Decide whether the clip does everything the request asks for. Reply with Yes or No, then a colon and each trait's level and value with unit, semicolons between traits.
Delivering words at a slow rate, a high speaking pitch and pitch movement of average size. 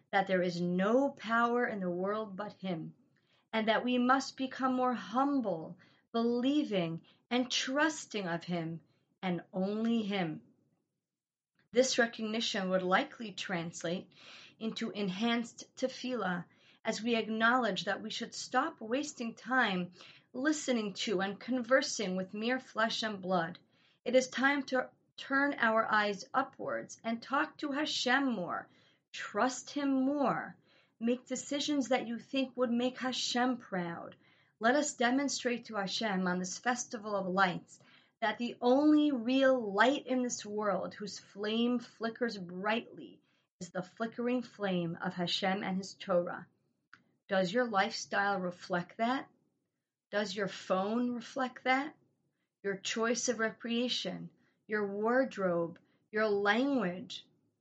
Yes: slow, 130 wpm; high, 230 Hz; average, 4.7 semitones